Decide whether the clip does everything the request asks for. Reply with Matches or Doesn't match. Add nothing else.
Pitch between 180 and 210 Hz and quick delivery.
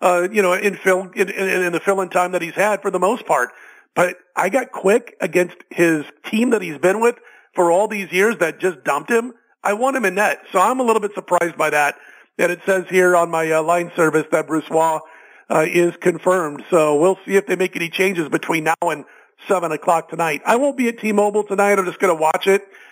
Matches